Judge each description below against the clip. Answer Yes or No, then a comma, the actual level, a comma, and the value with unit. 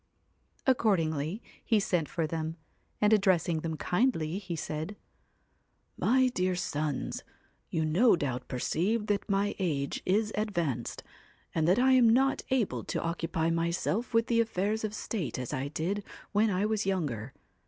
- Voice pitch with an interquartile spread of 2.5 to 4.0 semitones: No, average, 5.3 semitones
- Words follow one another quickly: No, average, 155 wpm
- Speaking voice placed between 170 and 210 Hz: Yes, medium, 185 Hz